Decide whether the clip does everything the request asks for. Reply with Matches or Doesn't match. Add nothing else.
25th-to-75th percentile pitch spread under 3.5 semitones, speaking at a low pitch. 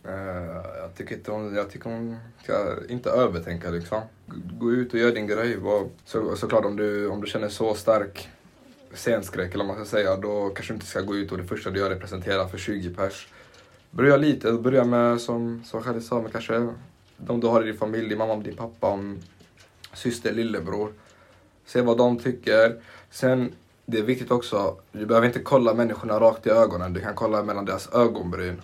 Matches